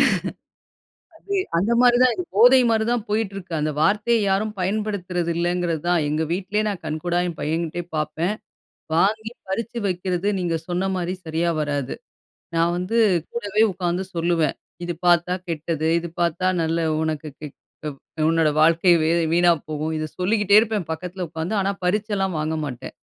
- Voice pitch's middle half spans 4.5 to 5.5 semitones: No, average, 3.8 semitones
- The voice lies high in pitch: No, medium, 175 Hz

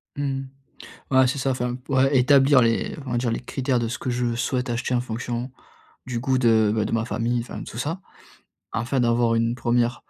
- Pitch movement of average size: No, narrow, 1.9 semitones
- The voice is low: Yes, low, 125 Hz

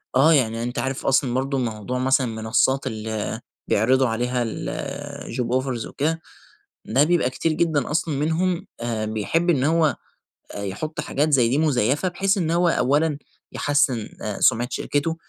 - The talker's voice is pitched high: No, low, 135 Hz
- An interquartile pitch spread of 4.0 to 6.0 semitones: Yes, average, 4.5 semitones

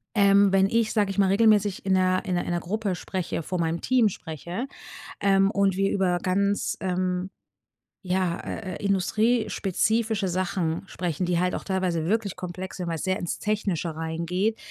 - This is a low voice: No, high, 190 Hz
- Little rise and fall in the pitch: Yes, narrow, 2.2 semitones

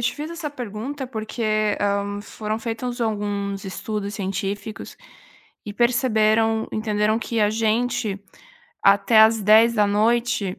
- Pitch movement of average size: No, narrow, 2.2 semitones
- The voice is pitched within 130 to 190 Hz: No, high, 215 Hz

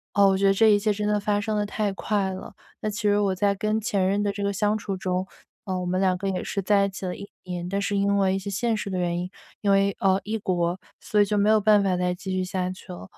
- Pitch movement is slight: Yes, narrow, 1.7 semitones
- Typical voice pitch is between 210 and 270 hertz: No, high, 200 Hz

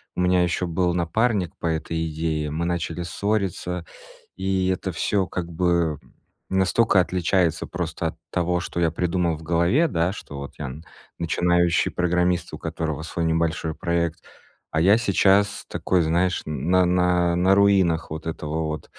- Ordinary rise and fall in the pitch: No, narrow, 2.0 semitones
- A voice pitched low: Yes, very low, 85 Hz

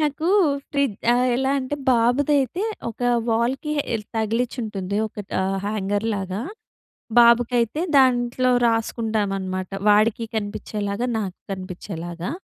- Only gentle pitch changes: No, average, 3.7 semitones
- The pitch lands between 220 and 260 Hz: Yes, high, 225 Hz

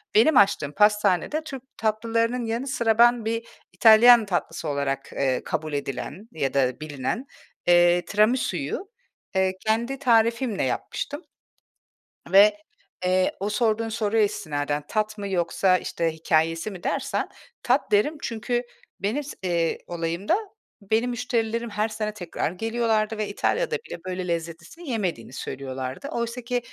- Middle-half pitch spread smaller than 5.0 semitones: No, wide, 5.4 semitones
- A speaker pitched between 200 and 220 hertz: Yes, high, 215 Hz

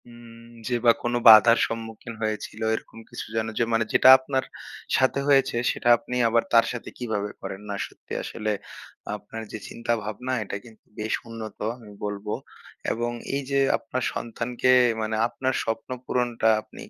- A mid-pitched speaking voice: No, low, 115 Hz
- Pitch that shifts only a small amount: Yes, narrow, 1.8 semitones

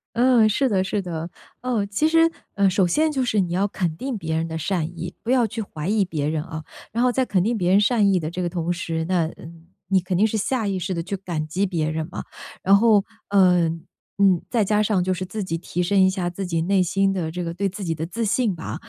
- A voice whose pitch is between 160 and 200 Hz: Yes, high, 190 Hz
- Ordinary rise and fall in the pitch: Yes, average, 3.6 semitones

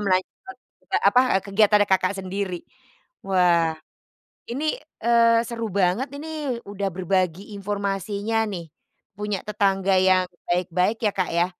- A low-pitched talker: No, high, 200 Hz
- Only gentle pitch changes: No, average, 3.1 semitones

